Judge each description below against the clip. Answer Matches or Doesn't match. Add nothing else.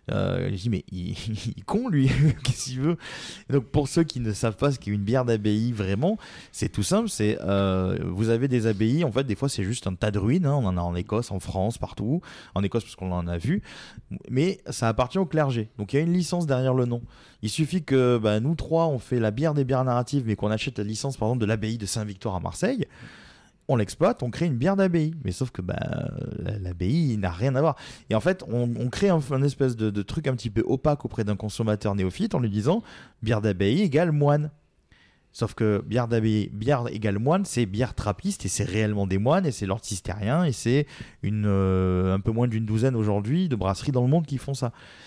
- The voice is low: Matches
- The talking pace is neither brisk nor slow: Doesn't match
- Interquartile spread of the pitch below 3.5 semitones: Doesn't match